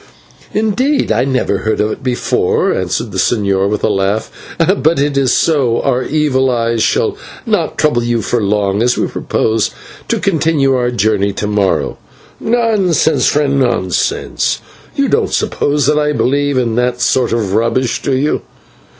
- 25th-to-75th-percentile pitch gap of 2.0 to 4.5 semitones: No, average, 4.9 semitones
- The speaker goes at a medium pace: Yes, average, 160 wpm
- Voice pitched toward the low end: Yes, low, 125 Hz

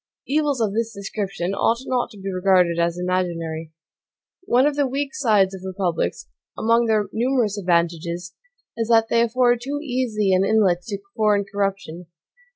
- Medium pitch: No, high, 205 Hz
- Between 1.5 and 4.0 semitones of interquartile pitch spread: No, average, 4.5 semitones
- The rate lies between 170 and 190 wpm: No, average, 160 wpm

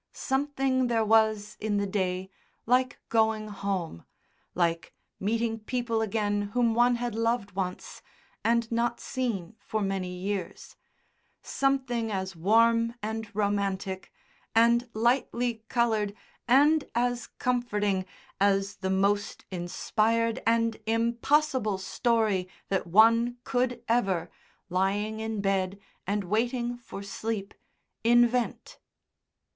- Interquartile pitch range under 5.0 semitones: Yes, average, 3.1 semitones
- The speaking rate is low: Yes, slow, 110 wpm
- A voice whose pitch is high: Yes, high, 220 Hz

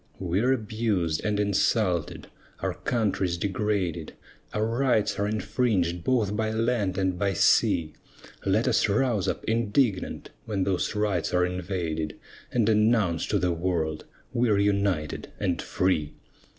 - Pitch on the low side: Yes, low, 100 Hz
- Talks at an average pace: No, slow, 130 wpm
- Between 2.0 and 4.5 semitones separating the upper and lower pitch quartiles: Yes, average, 3.5 semitones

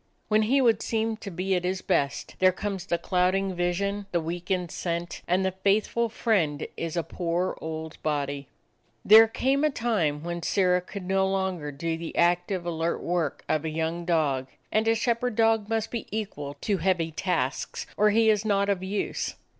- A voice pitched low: No, medium, 185 Hz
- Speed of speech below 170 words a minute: No, average, 185 wpm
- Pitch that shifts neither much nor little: Yes, average, 4.0 semitones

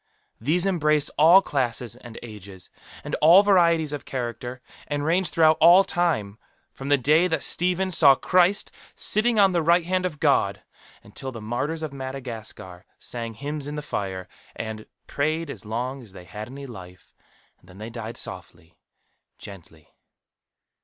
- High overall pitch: No, medium, 140 Hz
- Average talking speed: Yes, average, 160 wpm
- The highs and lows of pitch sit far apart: Yes, wide, 6.8 semitones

